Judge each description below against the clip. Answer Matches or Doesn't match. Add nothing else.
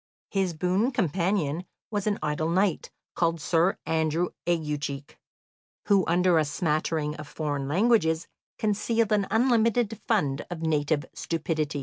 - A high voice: Doesn't match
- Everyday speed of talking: Doesn't match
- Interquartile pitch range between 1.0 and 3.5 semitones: Doesn't match